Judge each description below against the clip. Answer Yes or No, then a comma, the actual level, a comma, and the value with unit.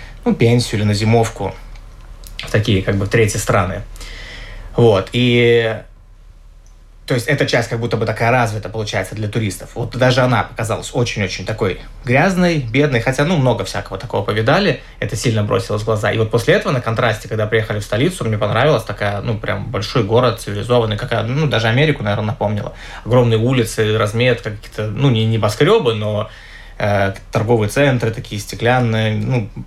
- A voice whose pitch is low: Yes, low, 115 Hz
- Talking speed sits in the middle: No, fast, 165 wpm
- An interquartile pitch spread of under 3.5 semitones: Yes, average, 2.8 semitones